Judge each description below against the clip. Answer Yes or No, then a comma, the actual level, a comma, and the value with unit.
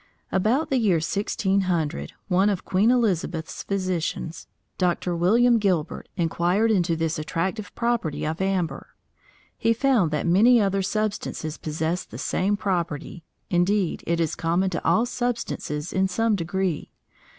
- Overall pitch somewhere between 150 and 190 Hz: Yes, medium, 185 Hz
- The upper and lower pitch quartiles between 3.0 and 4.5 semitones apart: Yes, average, 4.0 semitones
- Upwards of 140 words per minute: No, slow, 135 wpm